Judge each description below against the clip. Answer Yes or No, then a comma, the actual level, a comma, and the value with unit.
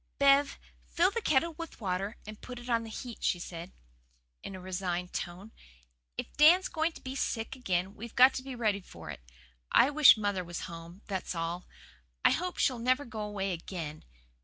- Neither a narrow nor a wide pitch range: No, wide, 6.5 semitones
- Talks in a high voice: Yes, high, 215 Hz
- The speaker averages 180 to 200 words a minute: Yes, average, 190 wpm